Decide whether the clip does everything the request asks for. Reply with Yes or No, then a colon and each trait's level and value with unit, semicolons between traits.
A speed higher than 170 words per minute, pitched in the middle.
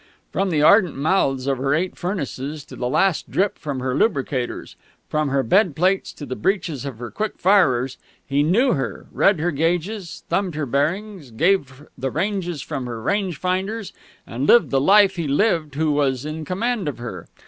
Yes: average, 185 wpm; medium, 155 Hz